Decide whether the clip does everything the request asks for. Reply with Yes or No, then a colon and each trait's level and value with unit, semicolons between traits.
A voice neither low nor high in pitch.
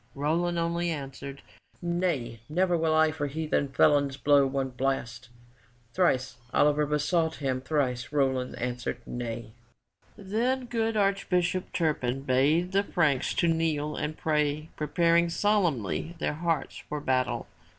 Yes: medium, 150 Hz